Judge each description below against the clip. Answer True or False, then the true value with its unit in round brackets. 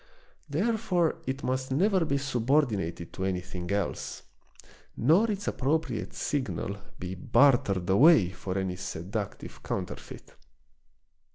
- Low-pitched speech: True (130 Hz)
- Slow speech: True (105 wpm)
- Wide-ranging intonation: True (8.4 semitones)